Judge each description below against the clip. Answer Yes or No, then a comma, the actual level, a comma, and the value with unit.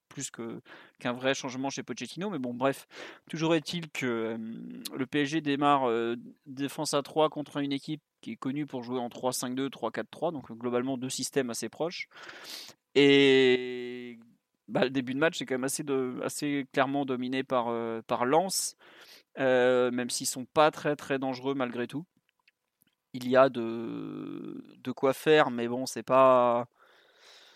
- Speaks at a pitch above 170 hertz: No, low, 135 Hz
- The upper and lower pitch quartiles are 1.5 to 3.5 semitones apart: Yes, average, 2.8 semitones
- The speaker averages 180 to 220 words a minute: No, average, 170 wpm